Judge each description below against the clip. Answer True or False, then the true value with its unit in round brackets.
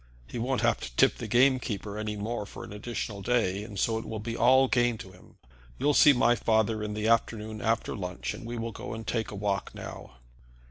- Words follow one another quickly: True (230 wpm)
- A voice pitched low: True (110 Hz)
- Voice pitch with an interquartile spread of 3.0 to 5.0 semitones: False (2.4 semitones)